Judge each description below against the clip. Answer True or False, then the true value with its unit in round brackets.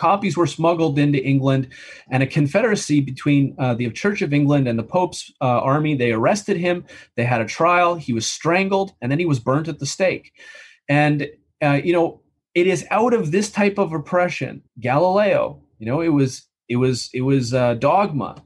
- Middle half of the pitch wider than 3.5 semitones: True (5.1 semitones)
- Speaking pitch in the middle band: True (145 Hz)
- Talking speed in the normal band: True (195 wpm)